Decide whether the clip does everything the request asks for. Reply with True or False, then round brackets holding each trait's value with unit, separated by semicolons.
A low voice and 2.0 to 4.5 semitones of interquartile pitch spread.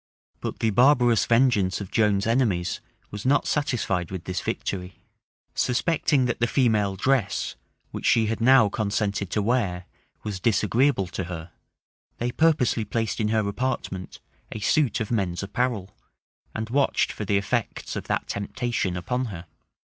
True (110 Hz; 3.9 semitones)